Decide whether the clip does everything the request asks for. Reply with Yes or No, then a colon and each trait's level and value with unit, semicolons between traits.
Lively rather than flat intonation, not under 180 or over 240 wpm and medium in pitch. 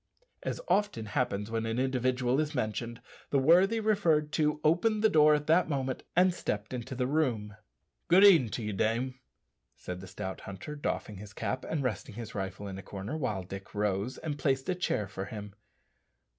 No: wide, 6.6 semitones; average, 185 wpm; low, 125 Hz